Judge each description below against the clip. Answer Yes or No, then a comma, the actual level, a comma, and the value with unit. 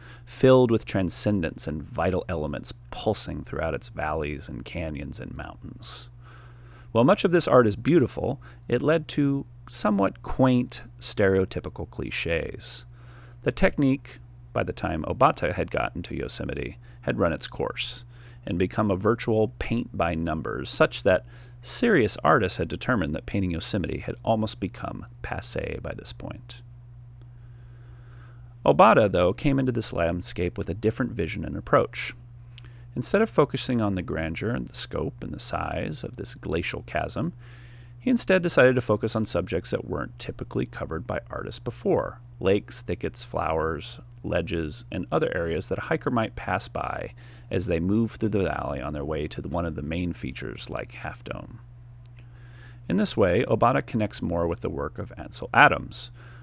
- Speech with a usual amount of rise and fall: Yes, average, 4.1 semitones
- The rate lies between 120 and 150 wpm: No, average, 160 wpm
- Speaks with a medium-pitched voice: No, low, 120 Hz